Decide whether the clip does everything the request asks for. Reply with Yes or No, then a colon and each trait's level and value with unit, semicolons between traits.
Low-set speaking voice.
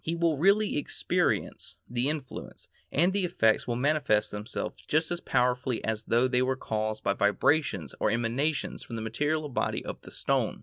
Yes: low, 130 Hz